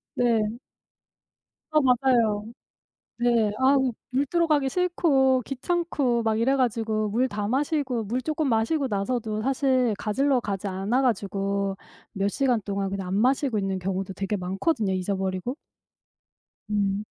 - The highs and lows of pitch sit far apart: No, average, 5.0 semitones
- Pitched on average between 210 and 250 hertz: Yes, high, 230 Hz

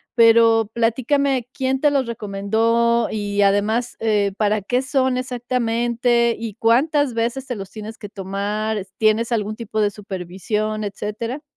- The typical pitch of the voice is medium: No, high, 225 Hz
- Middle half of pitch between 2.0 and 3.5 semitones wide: Yes, narrow, 2.6 semitones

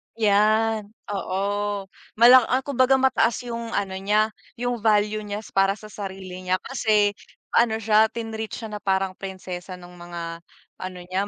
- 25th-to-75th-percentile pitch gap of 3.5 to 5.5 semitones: No, average, 2.8 semitones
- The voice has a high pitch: Yes, high, 210 Hz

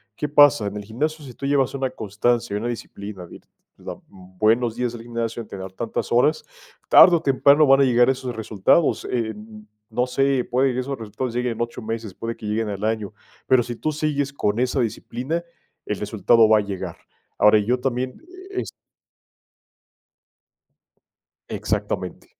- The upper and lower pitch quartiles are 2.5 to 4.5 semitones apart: Yes, average, 3.5 semitones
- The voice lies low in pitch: Yes, low, 120 Hz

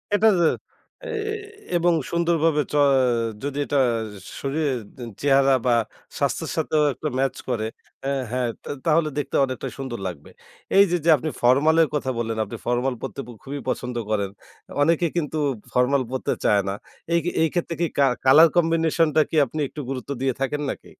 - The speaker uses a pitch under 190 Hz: Yes, medium, 140 Hz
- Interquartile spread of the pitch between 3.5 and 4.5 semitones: Yes, average, 4.0 semitones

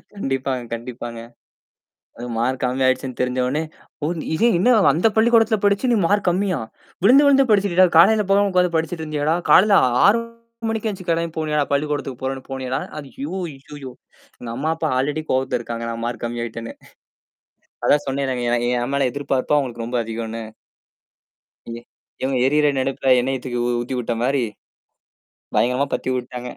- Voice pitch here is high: No, low, 135 Hz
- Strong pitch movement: Yes, wide, 6.1 semitones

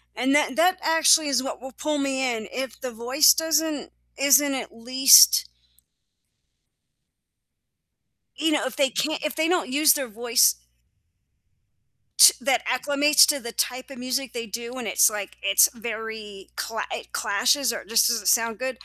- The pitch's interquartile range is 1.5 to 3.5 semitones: No, average, 3.9 semitones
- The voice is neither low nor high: No, very high, 255 Hz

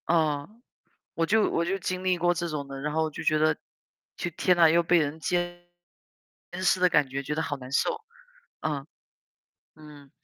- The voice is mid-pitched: Yes, medium, 160 Hz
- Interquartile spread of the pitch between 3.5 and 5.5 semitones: No, average, 2.9 semitones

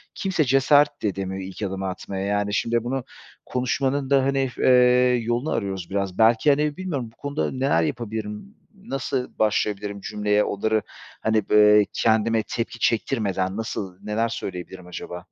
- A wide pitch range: No, average, 4.9 semitones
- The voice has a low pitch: Yes, low, 110 Hz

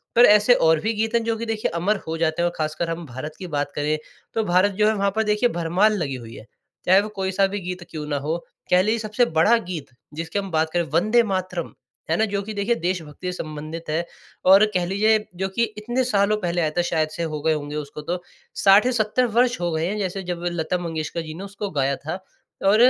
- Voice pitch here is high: No, medium, 180 Hz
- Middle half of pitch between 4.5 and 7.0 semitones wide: Yes, average, 4.8 semitones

